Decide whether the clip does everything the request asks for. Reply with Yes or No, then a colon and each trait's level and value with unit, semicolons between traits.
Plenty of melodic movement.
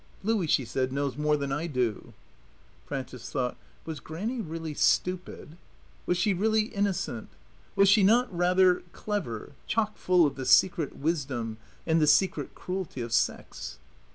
Yes: wide, 6.1 semitones